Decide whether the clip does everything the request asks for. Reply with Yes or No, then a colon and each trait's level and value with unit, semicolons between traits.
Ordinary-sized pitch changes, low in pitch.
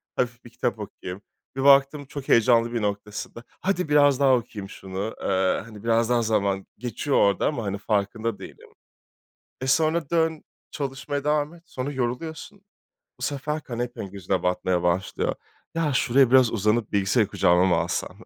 No: wide, 5.7 semitones; low, 120 Hz